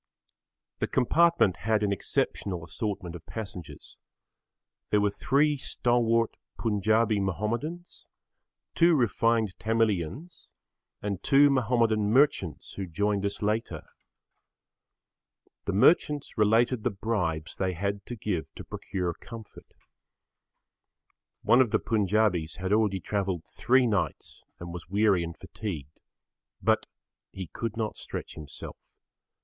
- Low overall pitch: Yes, low, 105 Hz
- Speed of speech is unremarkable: No, slow, 115 wpm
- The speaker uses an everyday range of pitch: Yes, average, 3.7 semitones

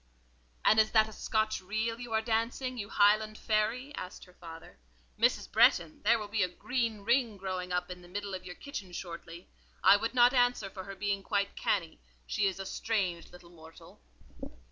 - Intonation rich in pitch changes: No, average, 3.6 semitones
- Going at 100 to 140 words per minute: No, average, 190 wpm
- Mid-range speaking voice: No, high, 205 Hz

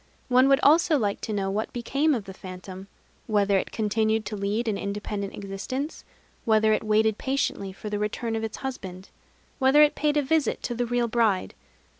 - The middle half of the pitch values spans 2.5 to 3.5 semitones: No, average, 4.2 semitones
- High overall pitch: Yes, high, 220 Hz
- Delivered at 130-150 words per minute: No, average, 190 wpm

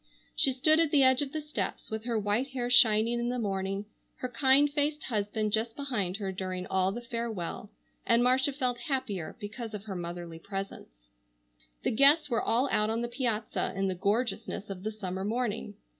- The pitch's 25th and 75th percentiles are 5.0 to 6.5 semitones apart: No, average, 4.3 semitones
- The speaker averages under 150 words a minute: No, average, 190 wpm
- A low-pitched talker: No, high, 225 Hz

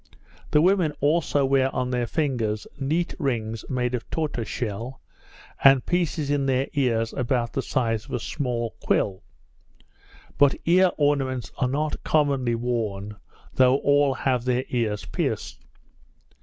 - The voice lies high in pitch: No, low, 130 Hz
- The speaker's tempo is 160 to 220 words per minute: No, average, 140 wpm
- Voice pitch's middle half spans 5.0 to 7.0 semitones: No, average, 3.4 semitones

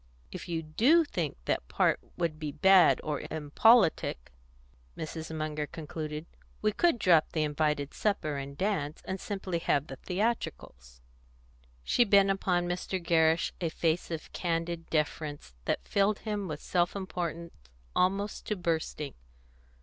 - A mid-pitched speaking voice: Yes, medium, 165 Hz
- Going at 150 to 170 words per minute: No, average, 140 wpm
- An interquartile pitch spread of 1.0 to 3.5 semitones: No, average, 4.0 semitones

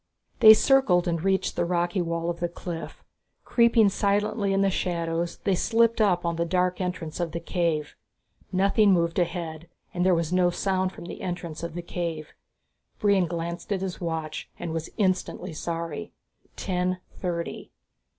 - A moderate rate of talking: Yes, average, 165 wpm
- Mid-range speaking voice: Yes, medium, 175 Hz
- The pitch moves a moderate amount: No, narrow, 2.3 semitones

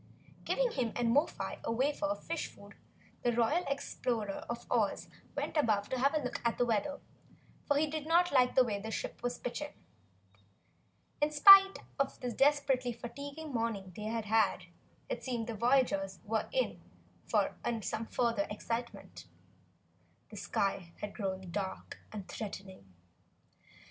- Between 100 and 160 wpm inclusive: Yes, average, 155 wpm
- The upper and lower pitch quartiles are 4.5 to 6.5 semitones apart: Yes, average, 5.0 semitones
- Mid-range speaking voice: No, high, 240 Hz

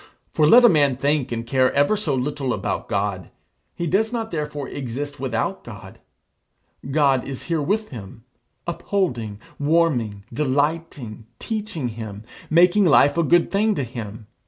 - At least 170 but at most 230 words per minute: No, average, 150 wpm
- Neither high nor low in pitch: Yes, medium, 145 Hz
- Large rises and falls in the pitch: Yes, wide, 5.9 semitones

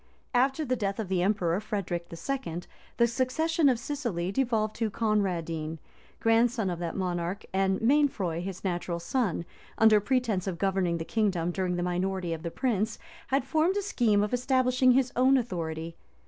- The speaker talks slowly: No, average, 165 wpm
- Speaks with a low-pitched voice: No, high, 205 Hz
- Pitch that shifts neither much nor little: No, wide, 6.1 semitones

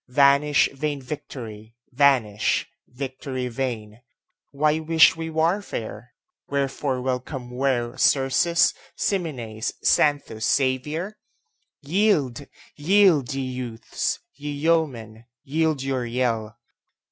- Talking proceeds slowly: Yes, slow, 90 wpm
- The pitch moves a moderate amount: Yes, average, 3.6 semitones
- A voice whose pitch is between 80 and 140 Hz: Yes, low, 135 Hz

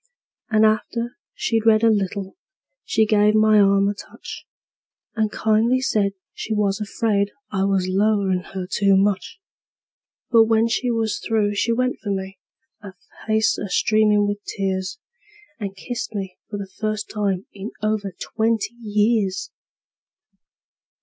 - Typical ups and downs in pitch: No, narrow, 1.9 semitones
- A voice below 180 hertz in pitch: No, high, 210 Hz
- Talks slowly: No, average, 145 wpm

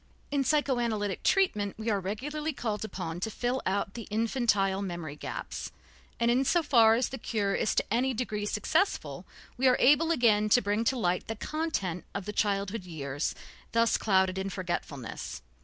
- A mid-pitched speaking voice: No, high, 215 Hz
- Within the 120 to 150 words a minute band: No, average, 175 wpm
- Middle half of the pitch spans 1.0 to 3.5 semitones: No, average, 4.5 semitones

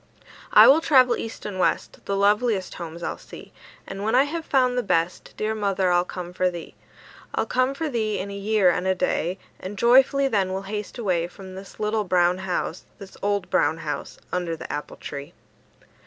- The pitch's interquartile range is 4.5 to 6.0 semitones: No, average, 3.7 semitones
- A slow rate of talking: No, average, 200 wpm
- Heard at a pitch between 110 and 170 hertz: No, high, 195 Hz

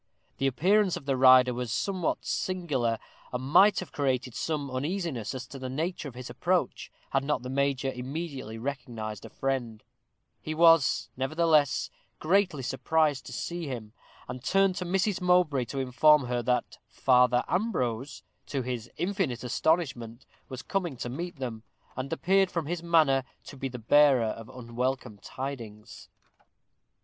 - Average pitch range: Yes, average, 4.7 semitones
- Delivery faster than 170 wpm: No, average, 155 wpm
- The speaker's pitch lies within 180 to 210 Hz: No, low, 135 Hz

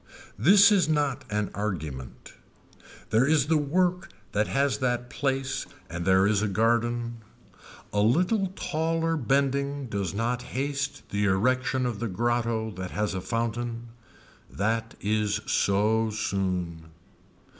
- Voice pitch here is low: Yes, low, 115 Hz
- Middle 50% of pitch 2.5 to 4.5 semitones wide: No, average, 5.1 semitones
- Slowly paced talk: Yes, slow, 130 wpm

